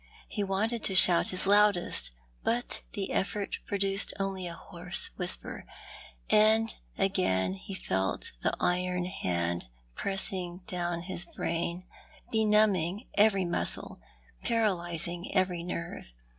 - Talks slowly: Yes, slow, 115 wpm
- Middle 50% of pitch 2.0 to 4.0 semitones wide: Yes, average, 2.7 semitones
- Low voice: No, medium, 185 Hz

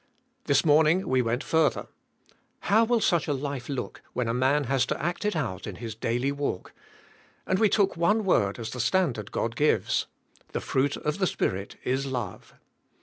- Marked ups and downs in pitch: Yes, wide, 5.9 semitones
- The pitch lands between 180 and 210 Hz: No, medium, 140 Hz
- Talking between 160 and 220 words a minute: Yes, average, 185 wpm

